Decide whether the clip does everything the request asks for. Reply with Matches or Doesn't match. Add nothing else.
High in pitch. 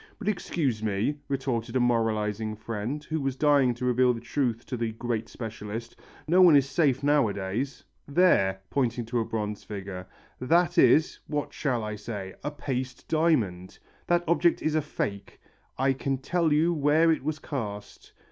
Doesn't match